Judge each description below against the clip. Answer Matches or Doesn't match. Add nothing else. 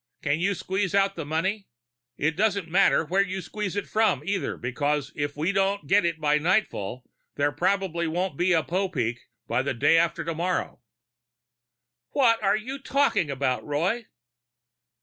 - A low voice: Doesn't match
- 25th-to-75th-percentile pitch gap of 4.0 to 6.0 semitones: Matches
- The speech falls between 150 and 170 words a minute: Matches